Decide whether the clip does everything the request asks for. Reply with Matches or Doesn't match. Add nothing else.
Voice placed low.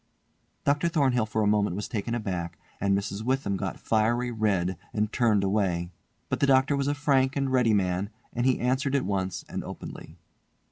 Matches